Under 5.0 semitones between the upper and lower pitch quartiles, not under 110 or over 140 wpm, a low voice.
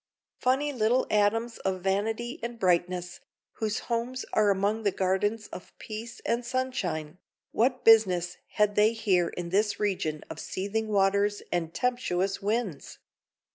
No: average, 3.7 semitones; slow, 135 wpm; high, 210 Hz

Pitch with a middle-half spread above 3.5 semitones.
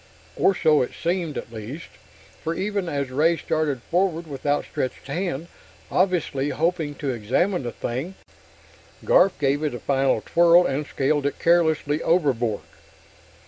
Yes: average, 4.1 semitones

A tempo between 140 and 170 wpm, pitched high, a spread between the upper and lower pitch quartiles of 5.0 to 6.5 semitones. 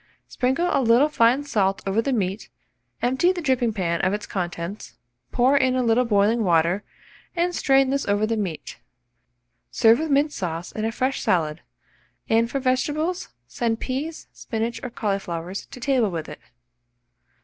Yes: average, 160 wpm; high, 230 Hz; wide, 5.4 semitones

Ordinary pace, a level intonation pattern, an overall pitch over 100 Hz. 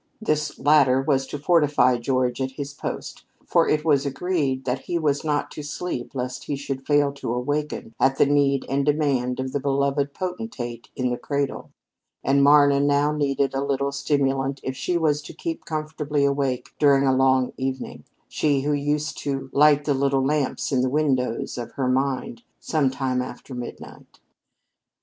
Yes: average, 175 wpm; narrow, 1.9 semitones; medium, 140 Hz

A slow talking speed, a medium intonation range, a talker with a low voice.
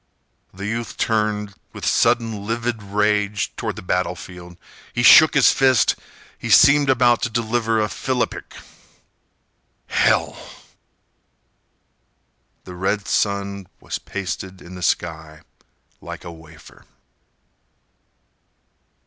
Yes: slow, 105 wpm; average, 4.1 semitones; low, 105 Hz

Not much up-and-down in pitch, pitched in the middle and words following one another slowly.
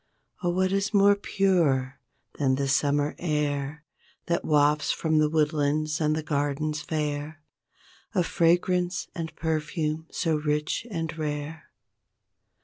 Yes: narrow, 2.3 semitones; medium, 155 Hz; slow, 120 wpm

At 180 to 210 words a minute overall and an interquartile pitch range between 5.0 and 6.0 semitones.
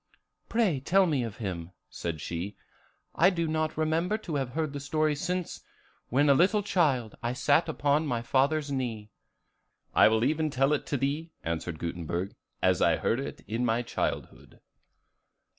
No: average, 165 wpm; wide, 5.6 semitones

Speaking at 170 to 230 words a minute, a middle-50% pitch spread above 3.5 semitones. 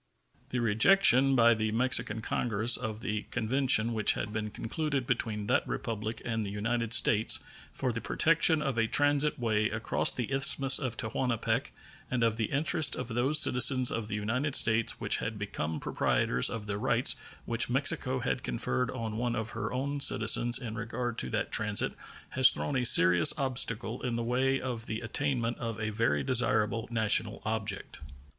No: average, 175 wpm; average, 2.9 semitones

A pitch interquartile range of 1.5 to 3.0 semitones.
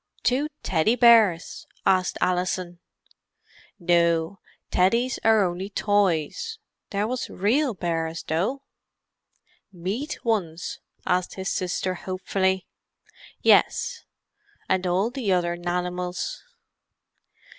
No: average, 4.0 semitones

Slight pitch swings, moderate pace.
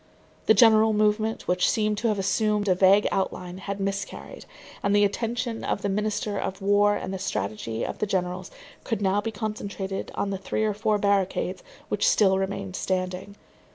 Yes: narrow, 1.8 semitones; average, 180 wpm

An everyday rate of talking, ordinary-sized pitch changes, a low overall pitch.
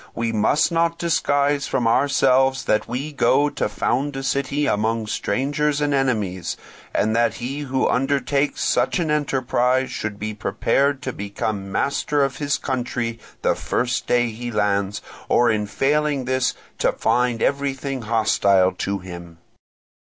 Yes: average, 145 wpm; average, 4.4 semitones; low, 125 Hz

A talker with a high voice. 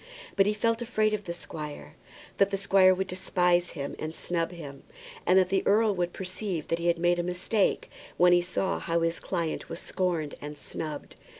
No: medium, 180 Hz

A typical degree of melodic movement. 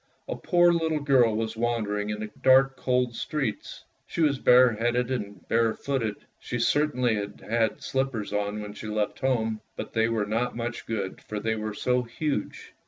Yes: average, 3.3 semitones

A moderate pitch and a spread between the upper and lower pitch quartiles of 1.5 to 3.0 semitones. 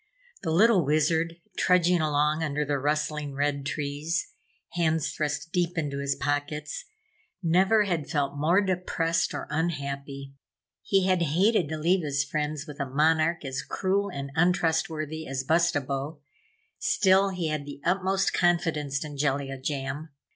No: medium, 155 Hz; average, 3.4 semitones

